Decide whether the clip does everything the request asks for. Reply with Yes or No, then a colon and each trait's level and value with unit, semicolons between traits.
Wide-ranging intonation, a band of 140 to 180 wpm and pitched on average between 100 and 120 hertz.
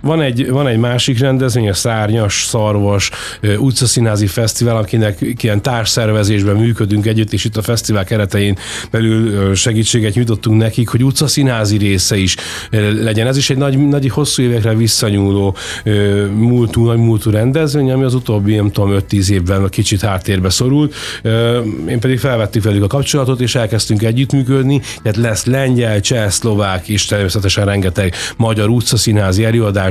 No: average, 2.9 semitones; average, 145 wpm; low, 110 Hz